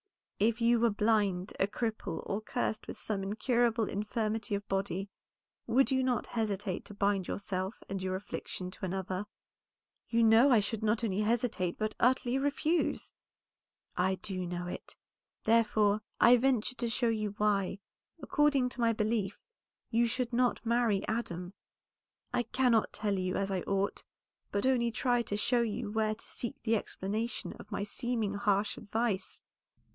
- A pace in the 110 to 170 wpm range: Yes, average, 160 wpm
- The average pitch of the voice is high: Yes, high, 215 Hz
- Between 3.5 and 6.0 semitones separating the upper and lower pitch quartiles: No, average, 3.1 semitones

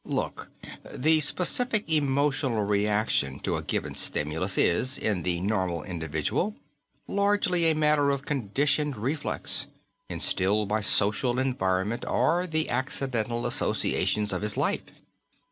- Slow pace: Yes, slow, 120 wpm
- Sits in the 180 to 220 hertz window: No, low, 120 Hz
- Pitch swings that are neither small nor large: No, wide, 6.8 semitones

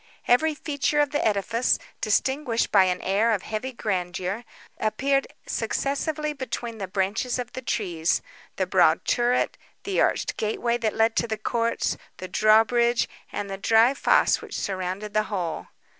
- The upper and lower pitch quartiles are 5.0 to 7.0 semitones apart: No, average, 4.1 semitones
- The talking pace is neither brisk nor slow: Yes, average, 150 wpm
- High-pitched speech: Yes, high, 225 Hz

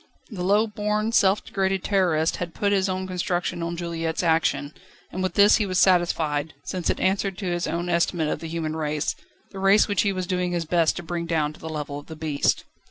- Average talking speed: No, fast, 225 wpm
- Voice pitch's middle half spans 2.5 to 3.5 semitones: Yes, average, 2.9 semitones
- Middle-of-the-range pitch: Yes, medium, 175 Hz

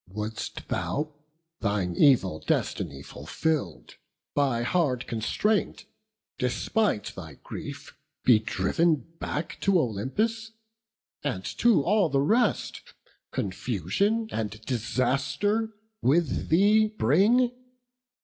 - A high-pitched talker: No, medium, 140 Hz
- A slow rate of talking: Yes, slow, 90 wpm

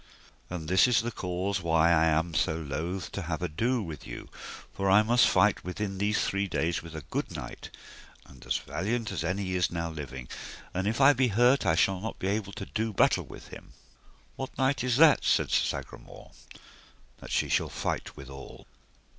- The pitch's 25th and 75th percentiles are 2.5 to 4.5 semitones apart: No, average, 5.0 semitones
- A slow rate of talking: No, average, 195 wpm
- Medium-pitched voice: No, very low, 95 Hz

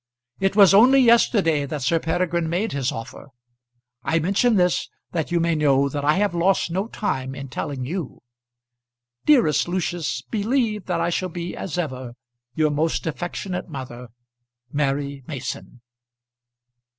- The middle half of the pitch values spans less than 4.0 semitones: No, average, 5.2 semitones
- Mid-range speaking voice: Yes, medium, 165 Hz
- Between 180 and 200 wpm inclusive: No, average, 145 wpm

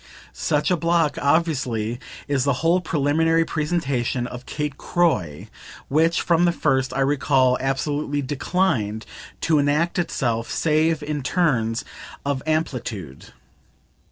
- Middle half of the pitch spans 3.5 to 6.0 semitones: Yes, average, 4.2 semitones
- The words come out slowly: Yes, slow, 120 wpm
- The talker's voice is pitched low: No, medium, 145 Hz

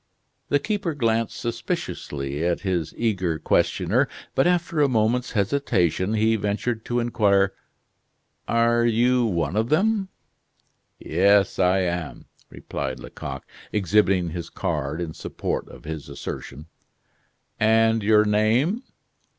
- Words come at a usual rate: No, slow, 120 wpm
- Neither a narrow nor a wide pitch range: Yes, average, 4.8 semitones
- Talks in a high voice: No, low, 110 Hz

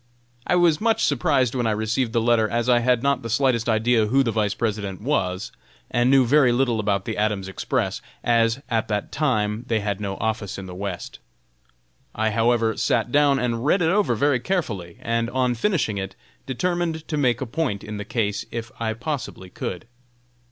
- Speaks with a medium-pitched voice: No, low, 115 Hz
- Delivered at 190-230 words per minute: Yes, average, 195 wpm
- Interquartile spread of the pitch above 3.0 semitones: Yes, average, 3.8 semitones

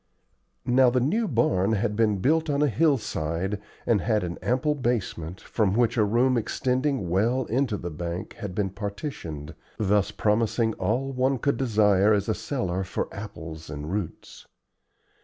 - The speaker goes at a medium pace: Yes, average, 160 wpm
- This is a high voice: No, low, 110 Hz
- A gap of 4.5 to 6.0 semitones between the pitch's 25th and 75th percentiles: Yes, average, 5.0 semitones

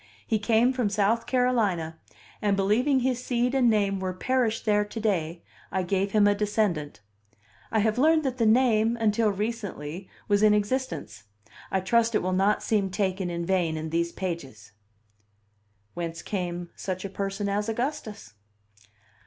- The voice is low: No, high, 205 Hz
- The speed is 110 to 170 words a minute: Yes, average, 160 wpm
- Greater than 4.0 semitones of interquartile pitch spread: No, average, 3.7 semitones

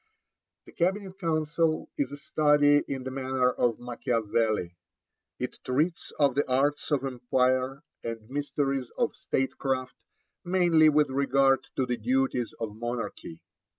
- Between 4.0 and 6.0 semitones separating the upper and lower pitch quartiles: No, average, 3.0 semitones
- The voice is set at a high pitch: No, low, 135 Hz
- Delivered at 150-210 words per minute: No, slow, 135 wpm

